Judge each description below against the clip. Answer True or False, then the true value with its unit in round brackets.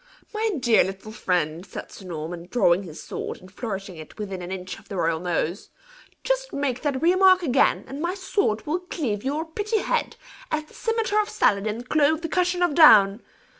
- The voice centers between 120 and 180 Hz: False (245 Hz)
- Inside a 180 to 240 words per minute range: True (190 wpm)